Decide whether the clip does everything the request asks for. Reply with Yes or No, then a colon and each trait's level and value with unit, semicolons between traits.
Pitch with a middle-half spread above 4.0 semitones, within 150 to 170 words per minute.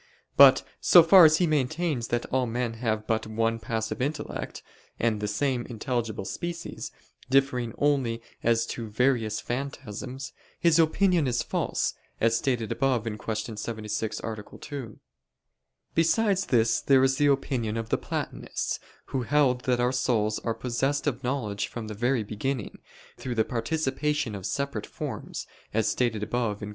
No: average, 3.7 semitones; average, 155 wpm